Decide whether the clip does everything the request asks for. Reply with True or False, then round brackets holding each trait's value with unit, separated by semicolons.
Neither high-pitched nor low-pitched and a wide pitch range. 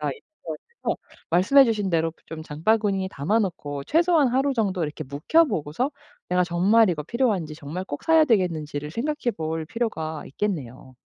True (180 Hz; 6.8 semitones)